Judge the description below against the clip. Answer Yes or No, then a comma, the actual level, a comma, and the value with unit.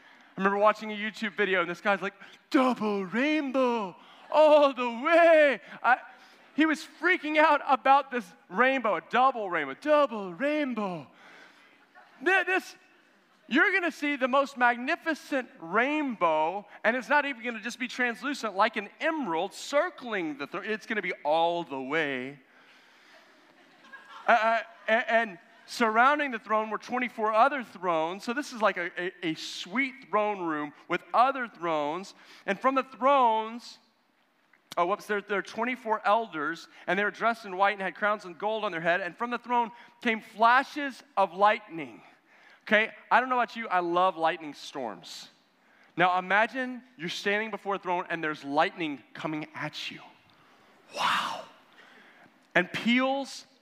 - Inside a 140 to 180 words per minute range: Yes, average, 155 wpm